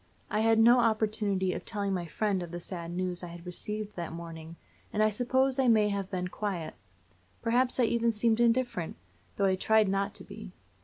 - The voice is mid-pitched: No, high, 205 Hz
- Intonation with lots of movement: No, average, 4.1 semitones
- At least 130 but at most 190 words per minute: No, average, 200 wpm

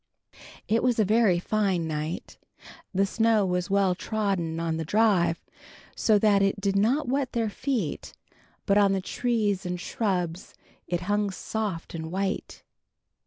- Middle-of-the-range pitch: No, high, 195 Hz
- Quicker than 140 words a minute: Yes, average, 155 wpm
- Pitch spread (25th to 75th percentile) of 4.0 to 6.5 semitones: No, average, 3.4 semitones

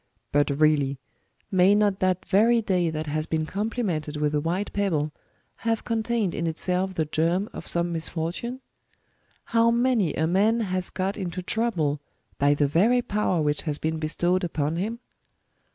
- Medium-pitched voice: Yes, medium, 180 Hz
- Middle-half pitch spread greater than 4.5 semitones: Yes, average, 5.1 semitones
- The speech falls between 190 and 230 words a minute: No, average, 165 wpm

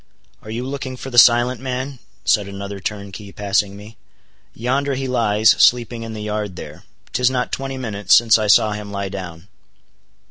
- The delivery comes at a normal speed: Yes, average, 170 wpm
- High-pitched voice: No, low, 110 Hz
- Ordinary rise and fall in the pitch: Yes, average, 3.7 semitones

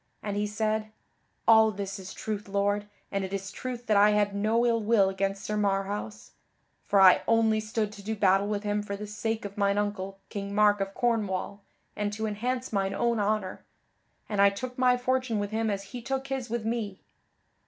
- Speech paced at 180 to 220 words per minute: Yes, average, 200 wpm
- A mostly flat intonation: Yes, narrow, 1.9 semitones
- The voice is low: No, high, 210 Hz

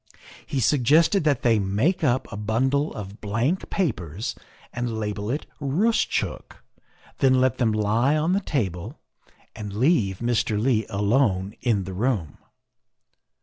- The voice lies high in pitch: No, low, 115 Hz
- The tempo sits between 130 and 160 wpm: Yes, average, 140 wpm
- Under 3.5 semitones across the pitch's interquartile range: No, average, 5.1 semitones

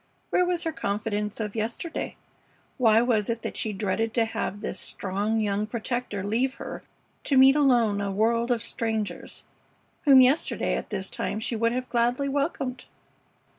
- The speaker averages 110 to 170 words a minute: Yes, average, 165 wpm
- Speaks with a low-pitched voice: No, high, 230 Hz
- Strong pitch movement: No, average, 3.3 semitones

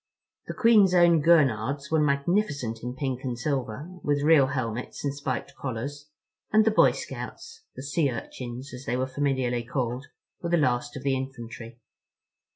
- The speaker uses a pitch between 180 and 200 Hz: No, low, 135 Hz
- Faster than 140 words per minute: Yes, average, 155 wpm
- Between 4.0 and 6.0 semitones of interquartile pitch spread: No, average, 3.4 semitones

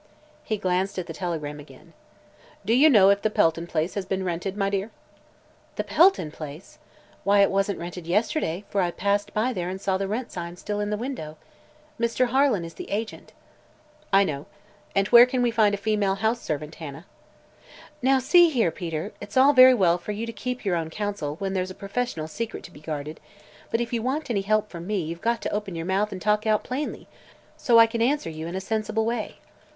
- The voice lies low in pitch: No, high, 200 Hz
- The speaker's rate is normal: No, fast, 215 wpm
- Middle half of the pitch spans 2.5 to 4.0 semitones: No, average, 4.8 semitones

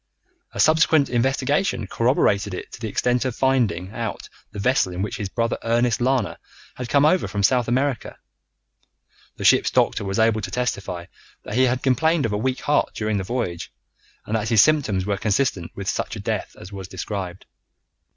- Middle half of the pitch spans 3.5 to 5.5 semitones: Yes, average, 4.6 semitones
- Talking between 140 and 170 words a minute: No, average, 185 wpm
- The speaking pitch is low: Yes, low, 115 Hz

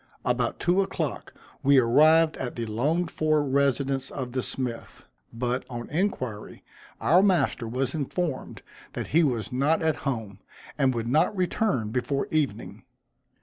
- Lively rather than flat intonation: No, average, 4.3 semitones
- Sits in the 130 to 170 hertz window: Yes, low, 135 Hz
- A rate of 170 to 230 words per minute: No, average, 145 wpm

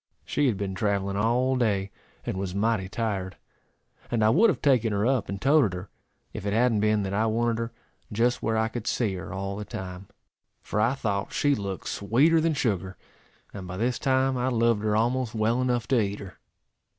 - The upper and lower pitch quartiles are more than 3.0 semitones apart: Yes, average, 3.7 semitones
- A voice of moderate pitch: No, low, 110 Hz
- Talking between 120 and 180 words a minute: No, fast, 205 wpm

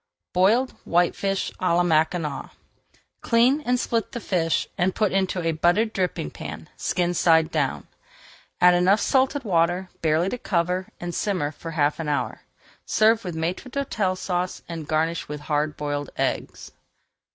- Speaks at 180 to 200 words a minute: No, average, 150 wpm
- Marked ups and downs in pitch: No, average, 3.6 semitones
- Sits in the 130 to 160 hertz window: No, medium, 175 Hz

